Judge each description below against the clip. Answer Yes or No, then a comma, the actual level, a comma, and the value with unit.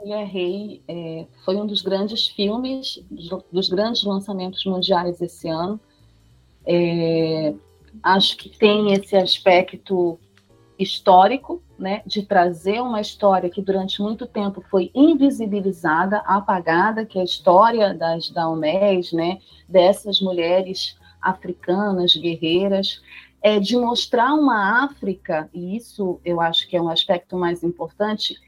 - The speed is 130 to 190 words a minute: No, slow, 120 wpm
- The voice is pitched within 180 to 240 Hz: Yes, high, 190 Hz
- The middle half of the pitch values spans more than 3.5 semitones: No, average, 3.2 semitones